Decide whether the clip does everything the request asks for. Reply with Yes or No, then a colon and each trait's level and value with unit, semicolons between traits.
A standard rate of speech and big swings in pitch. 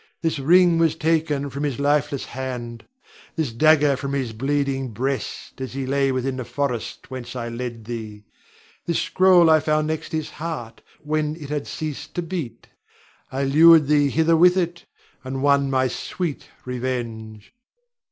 No: average, 160 wpm; average, 3.5 semitones